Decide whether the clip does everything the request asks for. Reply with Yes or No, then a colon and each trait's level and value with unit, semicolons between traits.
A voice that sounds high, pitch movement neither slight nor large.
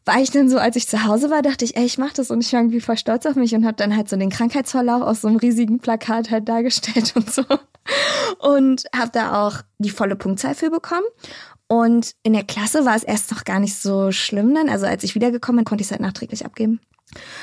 Yes: high, 230 Hz; average, 3.0 semitones